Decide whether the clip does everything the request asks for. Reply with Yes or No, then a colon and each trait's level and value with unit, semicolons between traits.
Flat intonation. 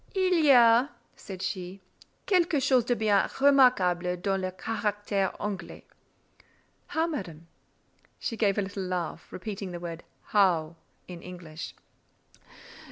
No: average, 5.1 semitones